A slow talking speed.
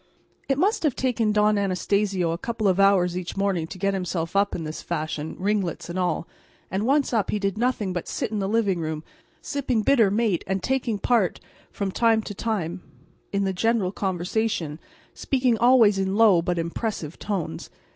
No: average, 185 wpm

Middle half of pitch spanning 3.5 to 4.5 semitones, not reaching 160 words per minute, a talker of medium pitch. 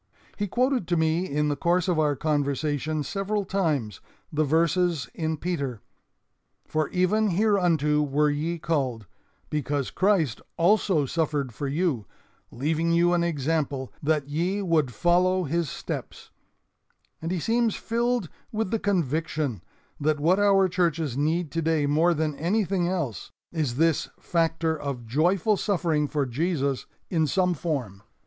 Yes: average, 3.8 semitones; average, 140 wpm; medium, 160 Hz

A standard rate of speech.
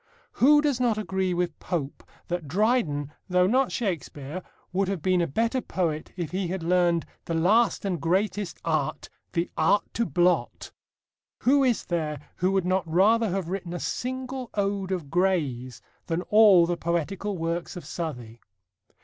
Yes: average, 160 wpm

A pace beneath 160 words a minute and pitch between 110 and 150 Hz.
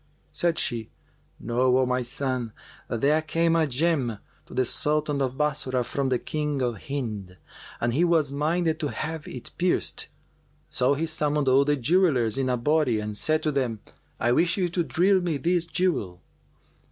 No: average, 175 wpm; medium, 140 Hz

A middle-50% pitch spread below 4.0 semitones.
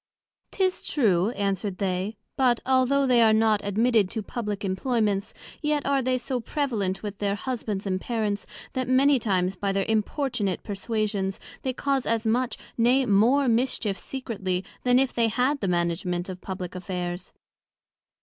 No: average, 4.7 semitones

